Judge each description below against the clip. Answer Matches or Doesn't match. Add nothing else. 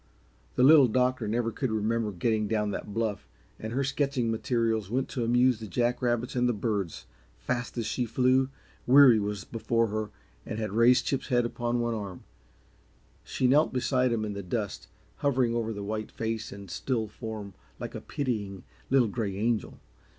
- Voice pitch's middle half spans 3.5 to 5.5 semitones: Doesn't match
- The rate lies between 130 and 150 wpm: Doesn't match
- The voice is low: Matches